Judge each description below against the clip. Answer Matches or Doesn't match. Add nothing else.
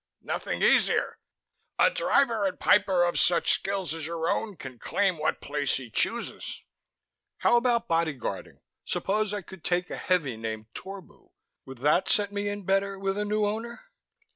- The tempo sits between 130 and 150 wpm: Doesn't match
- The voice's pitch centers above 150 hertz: Matches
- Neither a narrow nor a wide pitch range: Matches